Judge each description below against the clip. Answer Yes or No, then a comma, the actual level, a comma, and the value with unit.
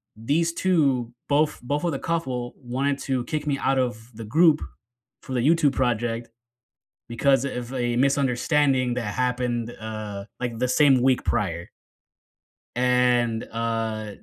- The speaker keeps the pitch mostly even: No, average, 3.0 semitones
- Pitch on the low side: Yes, low, 125 Hz